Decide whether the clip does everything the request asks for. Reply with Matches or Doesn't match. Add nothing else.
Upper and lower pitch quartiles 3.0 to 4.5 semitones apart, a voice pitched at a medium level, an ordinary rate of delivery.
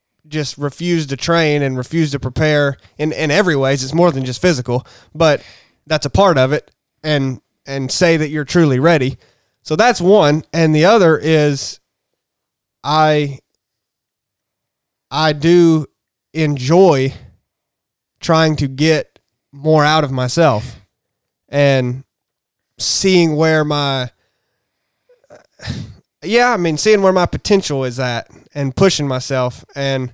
Doesn't match